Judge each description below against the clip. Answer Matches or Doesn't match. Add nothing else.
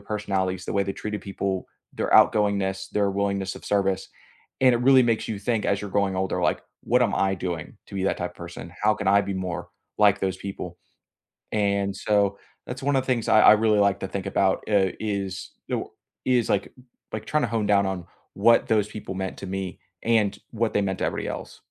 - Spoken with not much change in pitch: Matches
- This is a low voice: Matches